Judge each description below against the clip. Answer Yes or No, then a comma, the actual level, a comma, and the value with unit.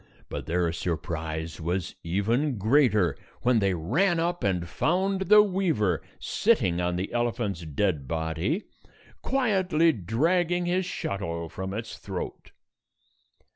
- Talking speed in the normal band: No, slow, 120 wpm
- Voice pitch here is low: Yes, low, 105 Hz